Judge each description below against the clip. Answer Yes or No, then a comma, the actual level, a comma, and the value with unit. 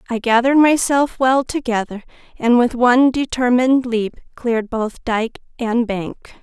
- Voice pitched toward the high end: Yes, high, 240 Hz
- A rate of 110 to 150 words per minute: Yes, average, 140 wpm